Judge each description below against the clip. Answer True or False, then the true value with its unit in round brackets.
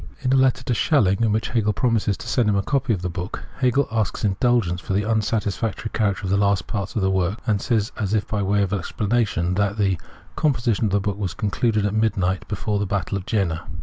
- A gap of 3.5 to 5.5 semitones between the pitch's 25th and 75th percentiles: False (2.7 semitones)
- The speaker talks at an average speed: False (240 wpm)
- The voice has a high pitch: False (105 Hz)